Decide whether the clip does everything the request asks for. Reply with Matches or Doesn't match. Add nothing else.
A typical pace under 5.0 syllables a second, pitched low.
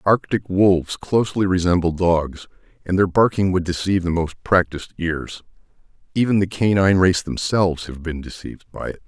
Doesn't match